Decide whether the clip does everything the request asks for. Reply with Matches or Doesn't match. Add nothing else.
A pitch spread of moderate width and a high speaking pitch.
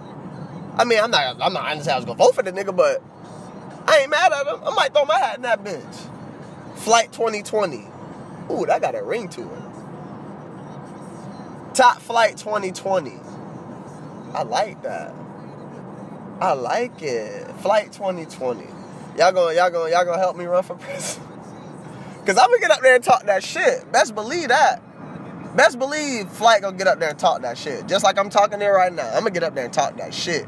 Doesn't match